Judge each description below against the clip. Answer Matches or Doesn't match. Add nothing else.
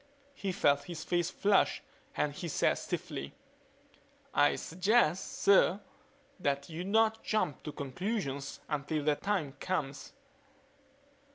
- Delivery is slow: Matches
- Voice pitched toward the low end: Doesn't match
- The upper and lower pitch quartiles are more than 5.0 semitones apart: Matches